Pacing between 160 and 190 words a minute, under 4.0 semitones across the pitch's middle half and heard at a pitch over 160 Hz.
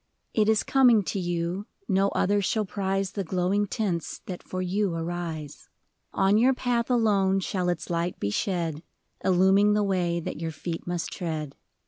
Yes: average, 165 wpm; average, 3.1 semitones; high, 190 Hz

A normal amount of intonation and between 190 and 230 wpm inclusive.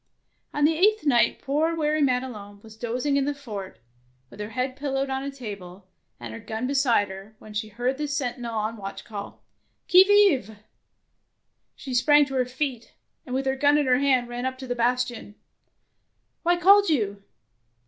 Yes: average, 4.5 semitones; average, 195 wpm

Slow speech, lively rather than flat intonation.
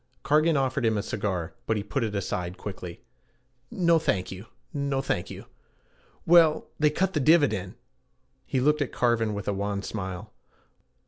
No: average, 165 wpm; wide, 7.0 semitones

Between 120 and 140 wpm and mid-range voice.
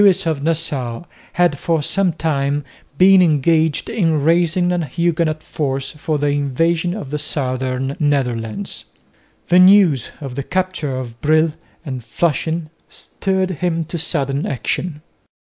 Yes: slow, 135 wpm; medium, 155 Hz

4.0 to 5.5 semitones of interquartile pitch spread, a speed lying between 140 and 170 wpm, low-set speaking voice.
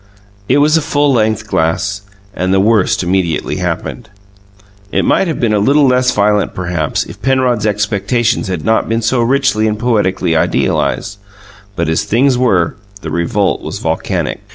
Yes: average, 5.0 semitones; average, 160 wpm; low, 105 Hz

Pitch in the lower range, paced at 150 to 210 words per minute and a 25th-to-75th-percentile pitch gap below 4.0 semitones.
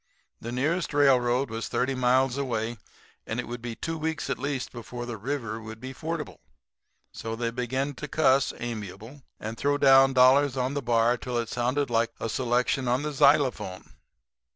Yes: low, 125 Hz; average, 175 wpm; average, 3.0 semitones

